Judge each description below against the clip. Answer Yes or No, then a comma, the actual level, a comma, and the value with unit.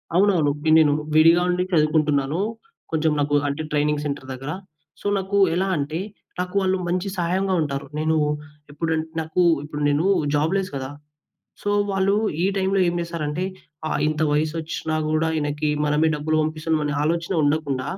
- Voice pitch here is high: No, medium, 155 Hz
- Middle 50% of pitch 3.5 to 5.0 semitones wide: No, average, 2.9 semitones